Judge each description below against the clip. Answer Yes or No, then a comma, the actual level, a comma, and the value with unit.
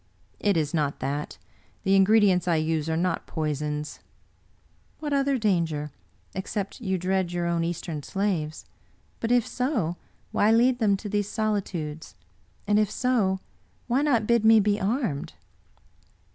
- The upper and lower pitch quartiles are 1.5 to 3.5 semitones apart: No, average, 5.3 semitones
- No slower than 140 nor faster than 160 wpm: Yes, average, 155 wpm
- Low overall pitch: No, high, 190 Hz